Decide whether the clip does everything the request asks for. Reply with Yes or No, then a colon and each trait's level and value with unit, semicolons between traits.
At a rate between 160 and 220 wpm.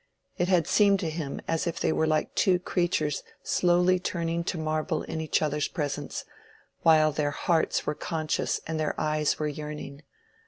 Yes: average, 170 wpm